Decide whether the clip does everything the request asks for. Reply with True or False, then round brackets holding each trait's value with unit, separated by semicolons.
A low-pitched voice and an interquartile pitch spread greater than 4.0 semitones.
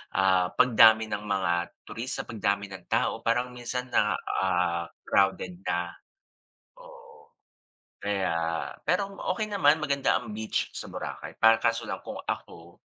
True (110 Hz; 5.1 semitones)